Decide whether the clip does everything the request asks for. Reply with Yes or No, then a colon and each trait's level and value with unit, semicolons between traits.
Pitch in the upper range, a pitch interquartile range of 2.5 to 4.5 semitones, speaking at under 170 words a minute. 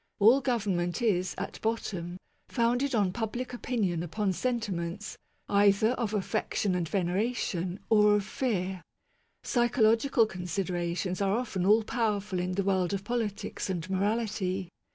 Yes: high, 200 Hz; average, 3.7 semitones; slow, 135 wpm